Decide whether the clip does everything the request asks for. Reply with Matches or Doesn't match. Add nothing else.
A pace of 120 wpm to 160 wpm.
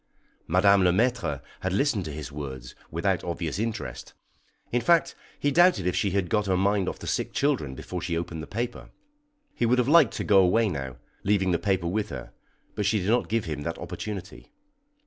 Doesn't match